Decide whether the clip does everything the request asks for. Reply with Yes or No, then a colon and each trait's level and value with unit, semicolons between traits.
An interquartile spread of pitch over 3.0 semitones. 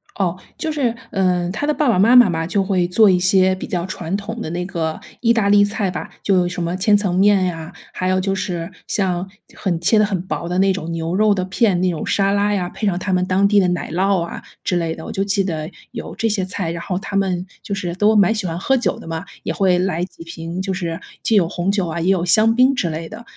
No: narrow, 2.6 semitones